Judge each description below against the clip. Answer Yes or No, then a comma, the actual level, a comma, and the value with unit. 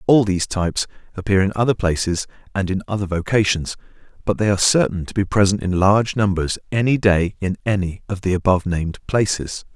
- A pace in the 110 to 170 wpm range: No, average, 185 wpm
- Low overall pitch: Yes, very low, 95 Hz